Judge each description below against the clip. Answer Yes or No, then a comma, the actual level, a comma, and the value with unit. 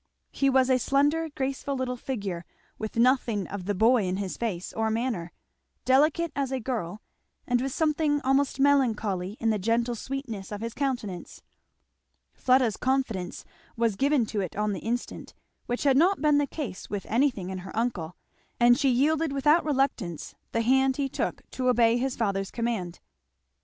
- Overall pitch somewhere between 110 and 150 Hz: No, high, 245 Hz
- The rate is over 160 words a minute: Yes, average, 170 wpm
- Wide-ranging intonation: No, average, 4.6 semitones